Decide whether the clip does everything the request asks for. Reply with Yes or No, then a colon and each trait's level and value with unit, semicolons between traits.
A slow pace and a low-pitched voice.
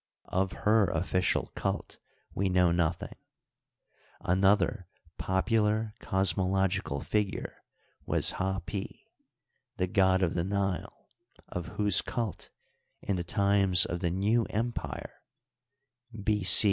Yes: slow, 110 wpm; very low, 95 Hz